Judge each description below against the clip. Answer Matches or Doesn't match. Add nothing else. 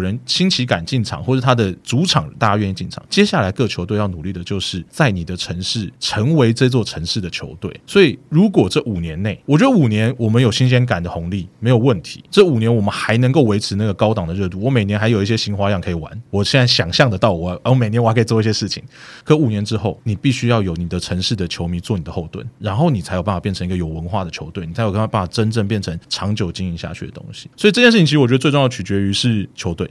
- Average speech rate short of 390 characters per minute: Doesn't match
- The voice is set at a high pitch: Doesn't match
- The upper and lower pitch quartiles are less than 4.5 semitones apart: Doesn't match